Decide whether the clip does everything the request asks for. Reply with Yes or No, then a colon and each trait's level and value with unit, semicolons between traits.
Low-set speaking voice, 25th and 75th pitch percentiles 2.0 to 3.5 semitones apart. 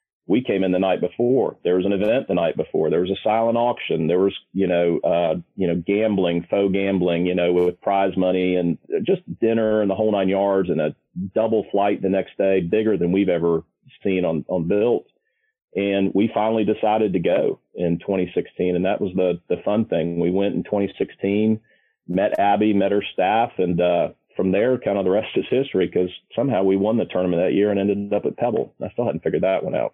Yes: low, 100 Hz; average, 2.9 semitones